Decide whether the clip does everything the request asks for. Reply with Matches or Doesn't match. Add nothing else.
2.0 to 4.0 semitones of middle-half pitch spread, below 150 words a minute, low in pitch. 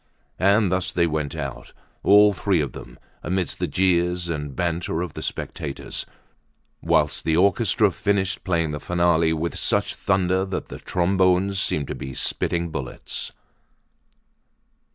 Matches